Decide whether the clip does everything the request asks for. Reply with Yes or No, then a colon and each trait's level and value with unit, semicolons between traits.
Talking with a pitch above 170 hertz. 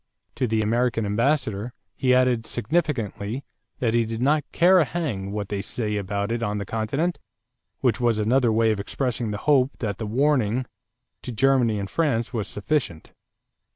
No: low, 115 Hz